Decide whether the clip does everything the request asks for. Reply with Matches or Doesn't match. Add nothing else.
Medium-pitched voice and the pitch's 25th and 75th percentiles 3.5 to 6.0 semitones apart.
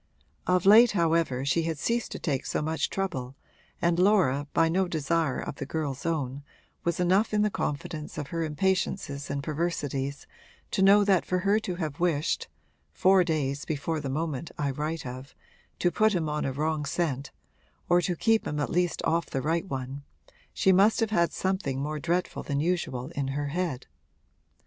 Matches